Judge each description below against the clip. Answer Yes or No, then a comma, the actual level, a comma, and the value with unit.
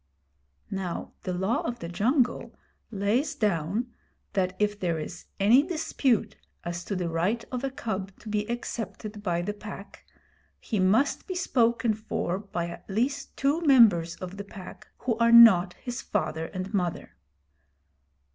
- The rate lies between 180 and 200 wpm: No, average, 155 wpm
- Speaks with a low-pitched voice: No, high, 210 Hz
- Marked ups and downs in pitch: No, average, 4.4 semitones